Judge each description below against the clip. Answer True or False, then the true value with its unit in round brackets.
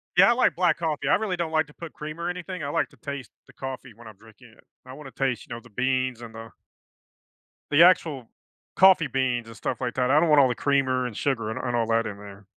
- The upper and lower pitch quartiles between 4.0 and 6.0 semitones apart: True (5.0 semitones)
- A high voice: False (130 Hz)